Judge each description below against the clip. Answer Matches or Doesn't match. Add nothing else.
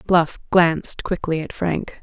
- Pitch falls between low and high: Matches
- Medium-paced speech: Matches